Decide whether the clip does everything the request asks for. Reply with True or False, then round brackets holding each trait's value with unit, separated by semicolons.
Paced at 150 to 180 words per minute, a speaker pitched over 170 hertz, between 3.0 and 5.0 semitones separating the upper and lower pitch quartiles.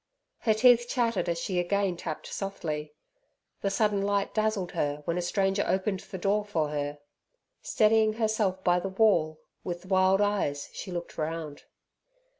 True (155 wpm; 190 Hz; 3.8 semitones)